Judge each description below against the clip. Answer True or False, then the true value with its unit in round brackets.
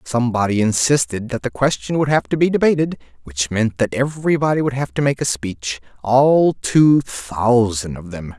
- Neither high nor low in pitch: False (125 Hz)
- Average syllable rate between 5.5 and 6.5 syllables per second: False (4.9 syllables/s)